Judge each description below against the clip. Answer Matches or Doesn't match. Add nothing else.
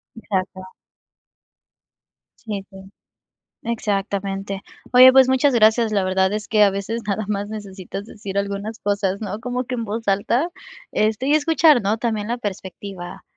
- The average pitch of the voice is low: Doesn't match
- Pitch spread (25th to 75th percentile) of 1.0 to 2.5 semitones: Doesn't match